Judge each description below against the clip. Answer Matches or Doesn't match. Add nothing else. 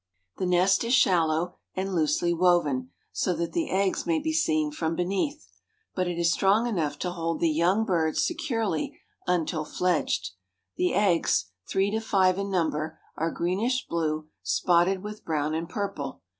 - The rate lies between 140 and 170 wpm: Matches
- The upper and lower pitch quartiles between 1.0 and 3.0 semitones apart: Doesn't match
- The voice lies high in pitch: Doesn't match